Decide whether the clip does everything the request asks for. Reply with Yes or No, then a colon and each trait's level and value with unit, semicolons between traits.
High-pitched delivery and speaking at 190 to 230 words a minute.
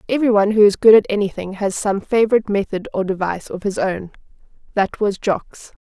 Yes: high, 200 Hz; average, 195 wpm